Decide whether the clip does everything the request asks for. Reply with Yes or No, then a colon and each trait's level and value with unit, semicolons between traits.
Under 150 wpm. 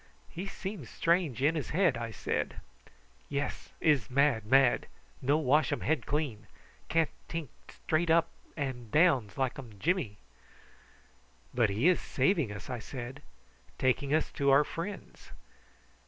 Yes: average, 140 wpm